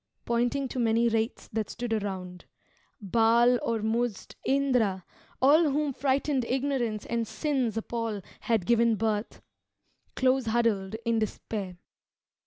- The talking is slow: Yes, slow, 115 wpm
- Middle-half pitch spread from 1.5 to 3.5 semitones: Yes, average, 2.8 semitones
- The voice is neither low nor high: No, high, 230 Hz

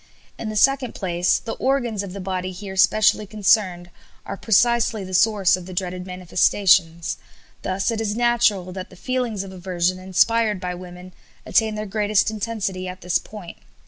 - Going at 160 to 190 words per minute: Yes, average, 170 wpm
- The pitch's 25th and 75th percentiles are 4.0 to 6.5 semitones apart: No, average, 3.0 semitones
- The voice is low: No, high, 195 Hz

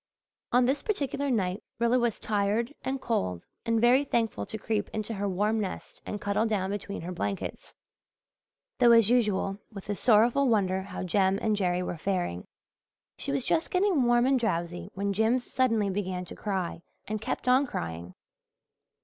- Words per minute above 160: Yes, average, 170 wpm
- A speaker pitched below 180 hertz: No, high, 210 Hz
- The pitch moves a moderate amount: Yes, average, 4.1 semitones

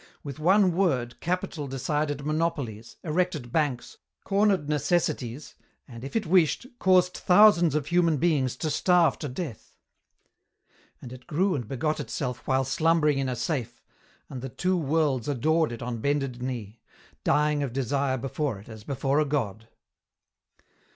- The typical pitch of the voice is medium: Yes, medium, 145 Hz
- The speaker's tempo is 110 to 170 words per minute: Yes, average, 150 wpm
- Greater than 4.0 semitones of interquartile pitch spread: Yes, average, 4.6 semitones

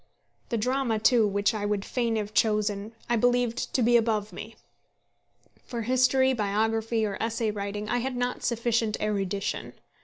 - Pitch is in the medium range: No, high, 225 Hz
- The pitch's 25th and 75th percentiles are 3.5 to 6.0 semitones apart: No, narrow, 2.5 semitones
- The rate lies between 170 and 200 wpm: No, average, 155 wpm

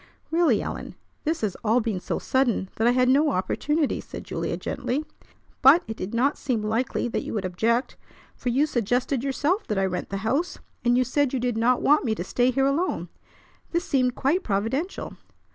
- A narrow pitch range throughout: No, average, 4.2 semitones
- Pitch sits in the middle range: No, very high, 250 Hz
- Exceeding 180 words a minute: Yes, average, 195 wpm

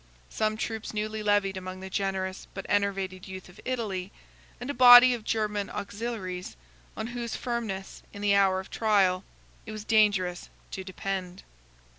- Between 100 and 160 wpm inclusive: Yes, average, 155 wpm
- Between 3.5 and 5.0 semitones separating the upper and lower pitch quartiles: No, narrow, 2.6 semitones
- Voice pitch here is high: Yes, high, 200 Hz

